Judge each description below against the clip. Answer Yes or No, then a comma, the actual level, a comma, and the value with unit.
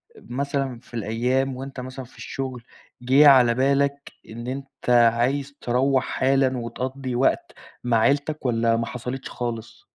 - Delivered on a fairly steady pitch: Yes, narrow, 2.3 semitones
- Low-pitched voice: Yes, low, 130 Hz